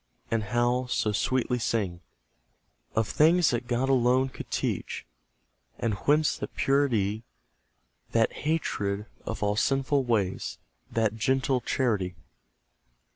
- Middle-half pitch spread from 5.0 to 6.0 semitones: No, average, 3.7 semitones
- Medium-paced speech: No, slow, 115 wpm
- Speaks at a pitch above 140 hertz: No, low, 120 Hz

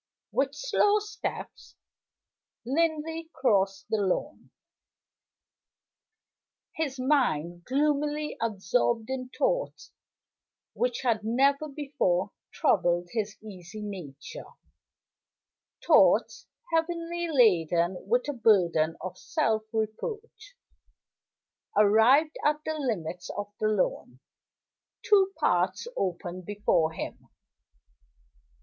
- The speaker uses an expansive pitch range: Yes, wide, 8.0 semitones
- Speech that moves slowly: Yes, slow, 90 wpm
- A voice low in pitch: No, high, 230 Hz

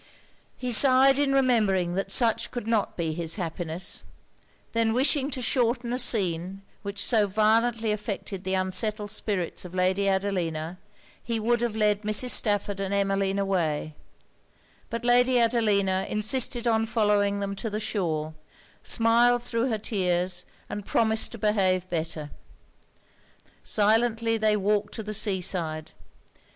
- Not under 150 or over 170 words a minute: No, average, 140 wpm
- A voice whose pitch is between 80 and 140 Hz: No, high, 210 Hz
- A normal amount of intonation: Yes, average, 3.5 semitones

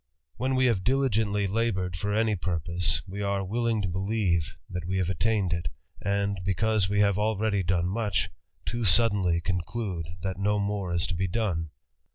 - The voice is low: Yes, low, 100 Hz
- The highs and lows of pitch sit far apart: No, average, 3.3 semitones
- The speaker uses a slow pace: No, average, 165 wpm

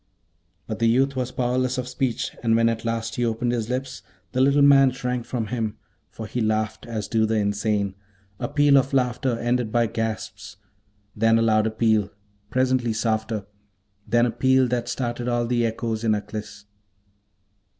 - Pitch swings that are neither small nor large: No, narrow, 2.3 semitones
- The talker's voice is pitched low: Yes, low, 115 Hz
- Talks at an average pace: Yes, average, 170 wpm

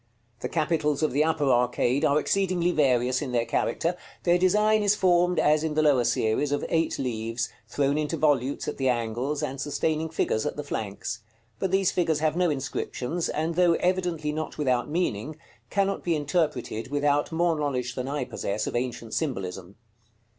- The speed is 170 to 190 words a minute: Yes, average, 175 wpm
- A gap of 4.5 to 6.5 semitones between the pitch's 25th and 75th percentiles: Yes, average, 4.8 semitones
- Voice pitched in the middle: Yes, medium, 150 Hz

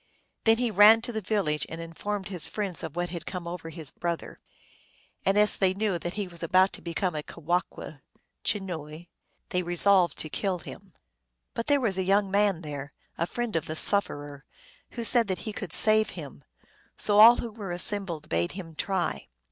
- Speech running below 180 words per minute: No, average, 190 wpm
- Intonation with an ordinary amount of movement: Yes, average, 3.8 semitones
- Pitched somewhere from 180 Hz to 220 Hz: Yes, medium, 185 Hz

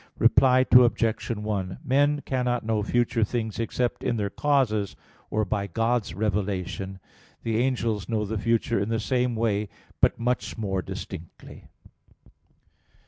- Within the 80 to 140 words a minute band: Yes, slow, 135 wpm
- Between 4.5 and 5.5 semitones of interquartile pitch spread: No, average, 3.0 semitones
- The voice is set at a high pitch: No, low, 110 Hz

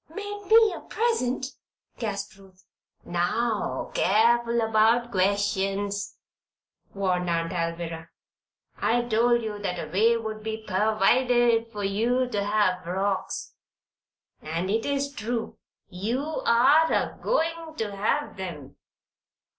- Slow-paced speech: Yes, slow, 115 wpm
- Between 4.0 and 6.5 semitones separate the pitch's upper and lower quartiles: No, average, 3.6 semitones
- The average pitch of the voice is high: Yes, high, 215 Hz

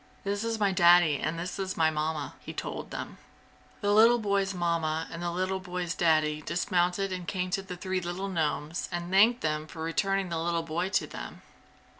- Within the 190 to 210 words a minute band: Yes, average, 195 wpm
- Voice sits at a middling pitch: Yes, medium, 175 Hz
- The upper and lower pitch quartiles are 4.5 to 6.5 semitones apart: No, average, 2.9 semitones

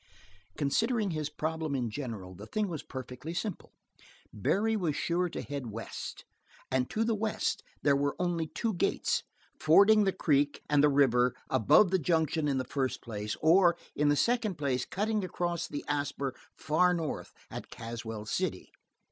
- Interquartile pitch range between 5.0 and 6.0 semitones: Yes, wide, 5.5 semitones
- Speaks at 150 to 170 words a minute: Yes, average, 165 wpm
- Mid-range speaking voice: Yes, medium, 150 Hz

